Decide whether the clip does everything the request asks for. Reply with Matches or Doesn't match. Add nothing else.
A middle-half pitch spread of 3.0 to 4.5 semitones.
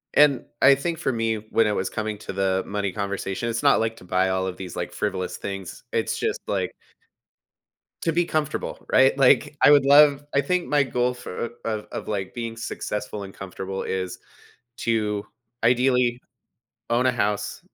Doesn't match